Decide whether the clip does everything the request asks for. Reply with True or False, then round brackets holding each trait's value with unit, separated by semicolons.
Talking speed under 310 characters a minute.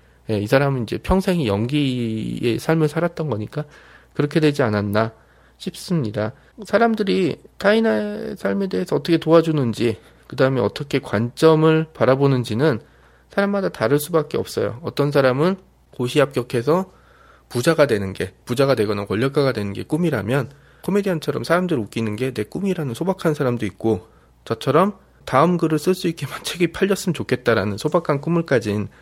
False (355 characters per minute)